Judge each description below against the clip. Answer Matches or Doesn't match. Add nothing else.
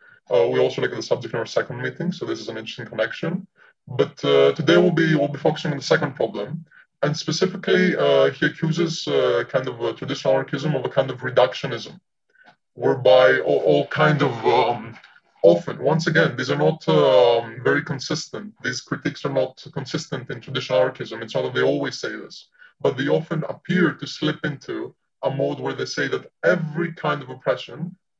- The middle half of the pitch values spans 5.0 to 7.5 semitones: Doesn't match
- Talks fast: Doesn't match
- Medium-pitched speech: Matches